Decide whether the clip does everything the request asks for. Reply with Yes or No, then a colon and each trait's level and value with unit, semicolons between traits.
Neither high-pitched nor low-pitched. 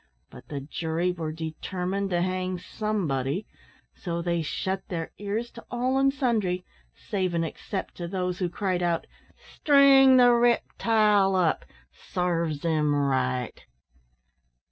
Yes: medium, 180 Hz